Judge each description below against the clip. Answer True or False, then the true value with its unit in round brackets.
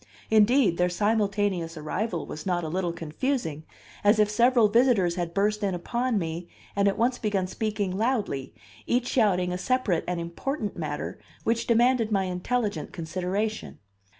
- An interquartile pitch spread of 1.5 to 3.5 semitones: False (4.4 semitones)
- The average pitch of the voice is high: True (200 Hz)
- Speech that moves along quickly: False (150 wpm)